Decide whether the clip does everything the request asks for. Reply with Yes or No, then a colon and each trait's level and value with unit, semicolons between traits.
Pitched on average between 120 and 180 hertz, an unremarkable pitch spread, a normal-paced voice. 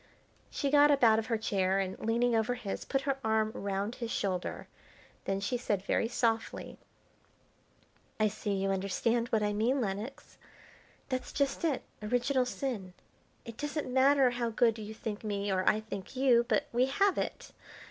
No: high, 225 Hz; average, 3.7 semitones; average, 170 wpm